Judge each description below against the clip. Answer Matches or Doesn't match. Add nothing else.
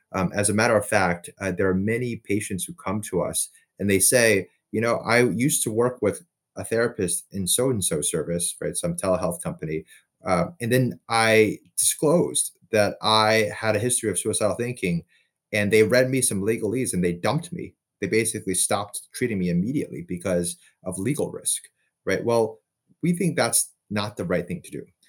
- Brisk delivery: Doesn't match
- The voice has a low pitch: Matches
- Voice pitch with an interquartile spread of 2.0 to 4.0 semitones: Doesn't match